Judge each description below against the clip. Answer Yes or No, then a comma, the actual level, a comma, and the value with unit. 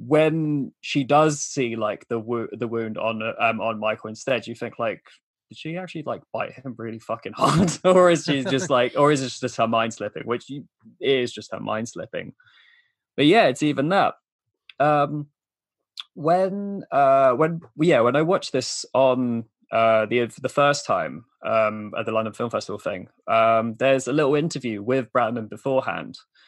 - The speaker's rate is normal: Yes, average, 180 wpm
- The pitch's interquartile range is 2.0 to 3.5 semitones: No, average, 4.9 semitones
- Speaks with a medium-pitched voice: No, low, 130 Hz